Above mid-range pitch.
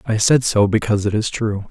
No: low, 110 Hz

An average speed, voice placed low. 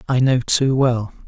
Yes: average, 190 wpm; low, 125 Hz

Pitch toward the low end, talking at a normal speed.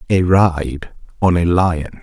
Yes: very low, 85 Hz; average, 150 wpm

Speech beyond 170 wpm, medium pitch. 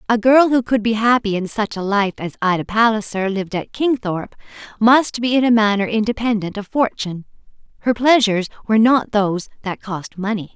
No: average, 180 wpm; high, 215 Hz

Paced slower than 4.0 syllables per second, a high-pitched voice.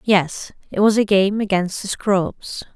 Yes: 3.7 syllables/s; high, 200 Hz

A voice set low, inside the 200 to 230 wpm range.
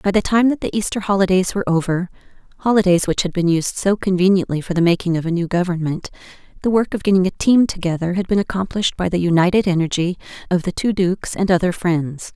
No: medium, 185 Hz; fast, 205 wpm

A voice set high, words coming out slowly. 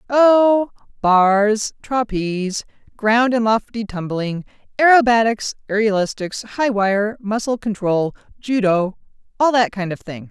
Yes: high, 215 Hz; slow, 105 wpm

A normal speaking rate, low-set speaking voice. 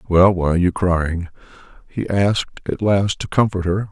Yes: average, 185 wpm; very low, 95 Hz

